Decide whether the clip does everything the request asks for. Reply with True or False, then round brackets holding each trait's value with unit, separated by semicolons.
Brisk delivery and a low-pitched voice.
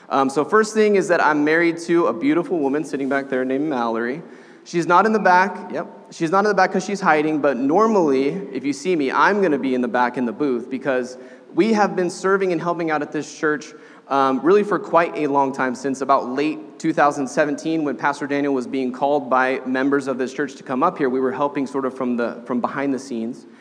False (240 wpm; 145 Hz)